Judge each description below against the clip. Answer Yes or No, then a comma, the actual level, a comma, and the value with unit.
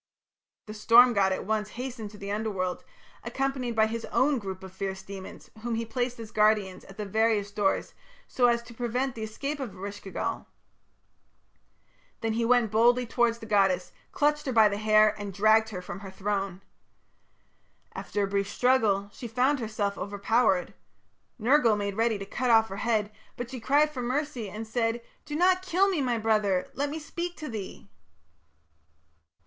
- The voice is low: No, high, 220 Hz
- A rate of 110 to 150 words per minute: No, average, 180 wpm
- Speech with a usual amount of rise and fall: Yes, average, 3.5 semitones